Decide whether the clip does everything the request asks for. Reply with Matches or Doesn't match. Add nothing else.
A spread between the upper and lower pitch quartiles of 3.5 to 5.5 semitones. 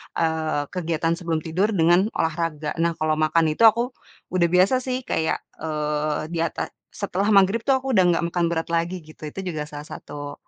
Doesn't match